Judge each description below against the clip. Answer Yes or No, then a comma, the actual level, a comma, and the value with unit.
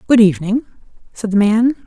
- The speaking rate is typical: Yes, average, 160 wpm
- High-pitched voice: Yes, high, 220 Hz